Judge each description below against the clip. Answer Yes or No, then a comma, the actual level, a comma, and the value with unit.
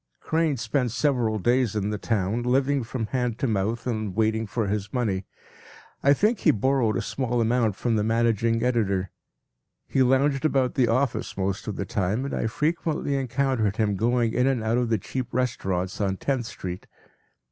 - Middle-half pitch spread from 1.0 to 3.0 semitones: No, average, 3.5 semitones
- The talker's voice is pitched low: Yes, low, 115 Hz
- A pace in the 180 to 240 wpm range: Yes, average, 185 wpm